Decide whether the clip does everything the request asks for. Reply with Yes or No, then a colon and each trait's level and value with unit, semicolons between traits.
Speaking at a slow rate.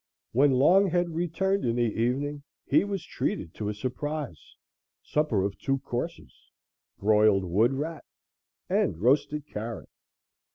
Yes: slow, 125 wpm